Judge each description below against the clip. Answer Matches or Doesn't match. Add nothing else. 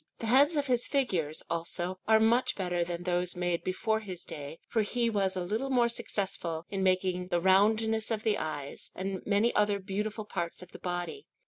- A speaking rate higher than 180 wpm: Matches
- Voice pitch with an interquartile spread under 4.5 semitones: Matches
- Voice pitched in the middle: Doesn't match